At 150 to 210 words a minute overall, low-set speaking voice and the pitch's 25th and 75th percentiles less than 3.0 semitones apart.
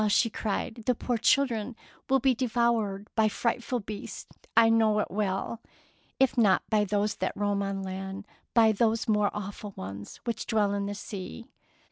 No: average, 180 wpm; high, 215 Hz; narrow, 2.6 semitones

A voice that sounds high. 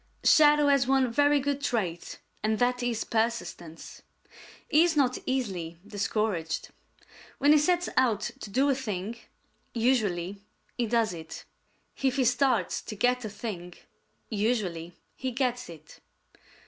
Yes: high, 235 Hz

